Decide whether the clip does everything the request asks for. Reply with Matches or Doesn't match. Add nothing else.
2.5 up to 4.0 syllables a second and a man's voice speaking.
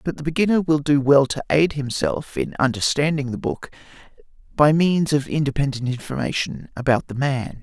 Doesn't match